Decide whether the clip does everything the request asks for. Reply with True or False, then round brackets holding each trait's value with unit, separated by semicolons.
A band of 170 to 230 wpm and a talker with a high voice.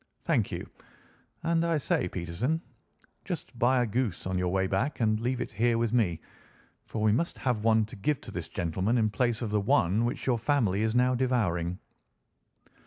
False (190 wpm; 115 Hz)